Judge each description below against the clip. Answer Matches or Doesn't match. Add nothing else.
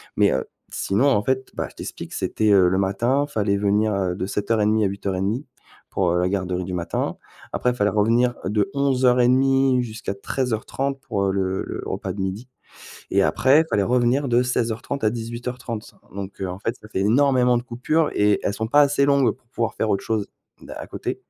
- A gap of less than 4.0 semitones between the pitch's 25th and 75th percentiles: Doesn't match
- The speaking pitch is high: Doesn't match